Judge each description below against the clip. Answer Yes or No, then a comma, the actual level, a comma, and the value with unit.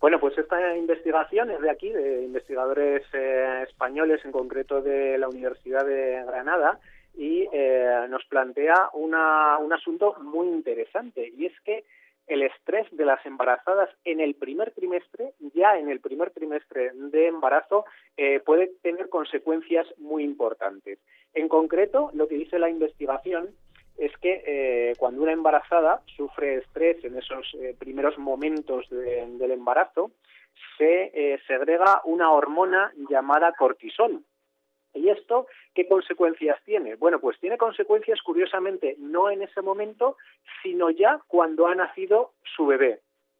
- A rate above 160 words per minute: No, average, 140 wpm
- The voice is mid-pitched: Yes, medium, 160 Hz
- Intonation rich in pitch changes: Yes, wide, 6.0 semitones